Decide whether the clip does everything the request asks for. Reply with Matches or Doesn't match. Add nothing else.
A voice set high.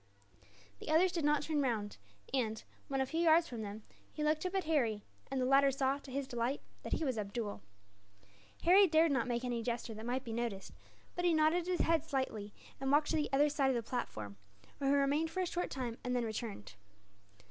Matches